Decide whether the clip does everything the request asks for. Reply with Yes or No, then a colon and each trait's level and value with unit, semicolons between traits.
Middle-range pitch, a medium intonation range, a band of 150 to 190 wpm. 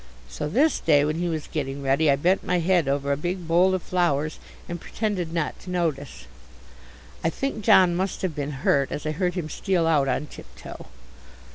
No: medium, 165 Hz; average, 3.8 semitones; average, 200 wpm